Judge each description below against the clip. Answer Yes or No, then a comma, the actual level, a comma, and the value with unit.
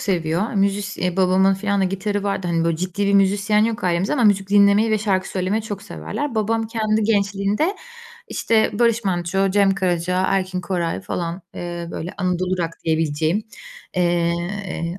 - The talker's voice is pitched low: No, high, 195 Hz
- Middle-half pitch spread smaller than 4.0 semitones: Yes, average, 2.7 semitones